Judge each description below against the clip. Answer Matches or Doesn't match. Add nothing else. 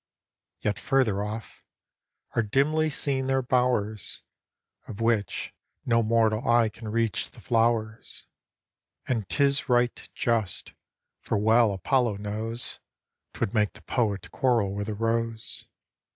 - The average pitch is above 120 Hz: Doesn't match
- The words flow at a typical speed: Doesn't match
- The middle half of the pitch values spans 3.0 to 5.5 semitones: Doesn't match